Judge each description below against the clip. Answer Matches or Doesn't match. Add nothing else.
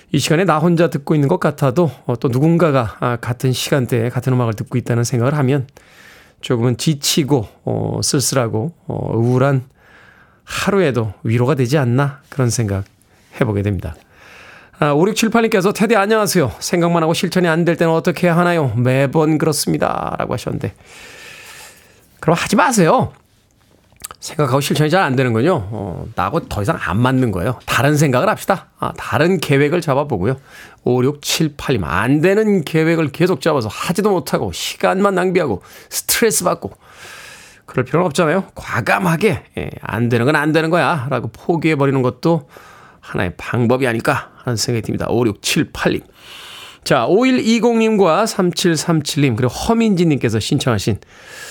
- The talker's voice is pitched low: Doesn't match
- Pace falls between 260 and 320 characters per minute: Matches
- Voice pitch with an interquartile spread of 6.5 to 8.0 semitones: Doesn't match